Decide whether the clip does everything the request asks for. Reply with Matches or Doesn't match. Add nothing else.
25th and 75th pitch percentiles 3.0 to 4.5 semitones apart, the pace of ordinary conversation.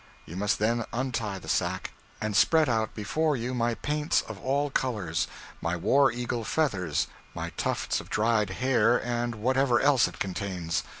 Matches